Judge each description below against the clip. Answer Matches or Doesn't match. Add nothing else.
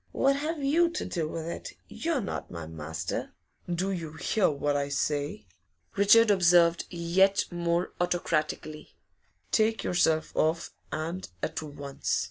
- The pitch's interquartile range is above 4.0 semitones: Matches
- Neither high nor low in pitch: Matches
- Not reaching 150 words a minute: Matches